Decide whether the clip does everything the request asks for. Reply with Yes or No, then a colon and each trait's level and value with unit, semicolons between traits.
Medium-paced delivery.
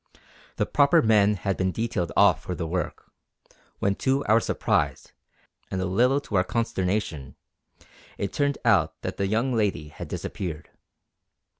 Yes: average, 150 wpm